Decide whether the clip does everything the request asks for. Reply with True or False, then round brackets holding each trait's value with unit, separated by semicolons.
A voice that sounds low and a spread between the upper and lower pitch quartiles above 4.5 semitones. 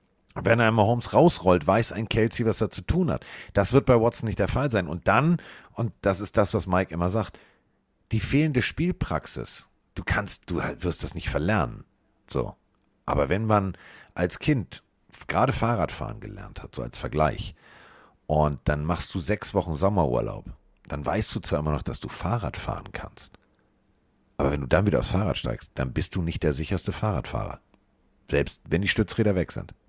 True (100 Hz; 5.0 semitones)